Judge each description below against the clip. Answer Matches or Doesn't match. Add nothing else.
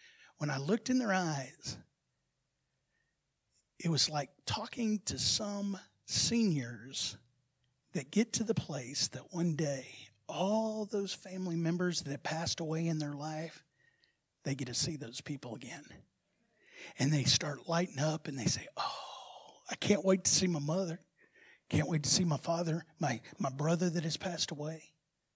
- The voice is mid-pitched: Matches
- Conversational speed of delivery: Matches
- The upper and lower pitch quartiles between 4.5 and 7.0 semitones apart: Matches